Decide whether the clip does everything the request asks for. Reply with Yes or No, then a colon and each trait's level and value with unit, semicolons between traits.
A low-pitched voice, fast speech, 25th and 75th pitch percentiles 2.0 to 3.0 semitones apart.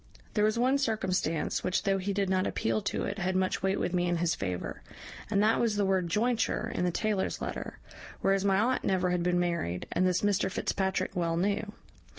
No: high, 190 Hz; fast, 210 wpm; narrow, 2.6 semitones